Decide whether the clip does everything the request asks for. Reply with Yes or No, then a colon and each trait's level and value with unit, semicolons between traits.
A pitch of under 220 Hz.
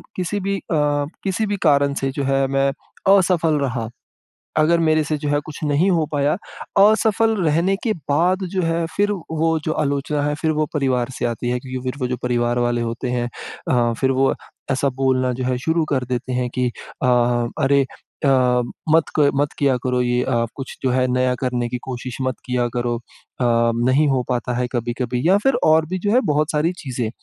Yes: medium, 140 Hz